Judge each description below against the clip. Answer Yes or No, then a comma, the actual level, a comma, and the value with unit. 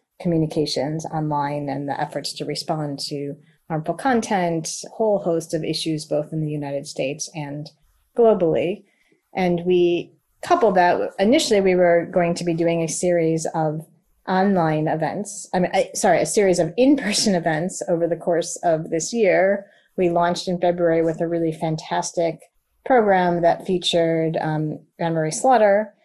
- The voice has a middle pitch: Yes, medium, 170 Hz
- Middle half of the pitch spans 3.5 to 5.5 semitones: No, average, 2.8 semitones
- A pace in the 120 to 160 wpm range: Yes, average, 155 wpm